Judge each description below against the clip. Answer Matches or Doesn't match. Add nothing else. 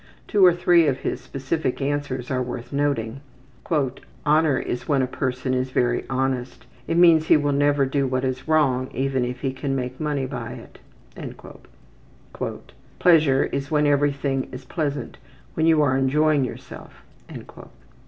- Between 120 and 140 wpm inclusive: Doesn't match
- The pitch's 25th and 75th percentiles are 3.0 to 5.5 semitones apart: Doesn't match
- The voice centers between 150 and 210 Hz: Doesn't match